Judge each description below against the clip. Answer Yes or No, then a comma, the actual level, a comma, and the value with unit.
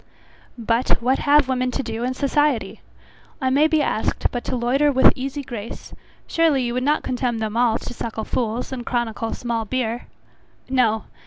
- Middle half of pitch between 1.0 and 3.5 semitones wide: Yes, narrow, 2.5 semitones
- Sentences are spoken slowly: No, average, 175 wpm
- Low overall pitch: No, very high, 250 Hz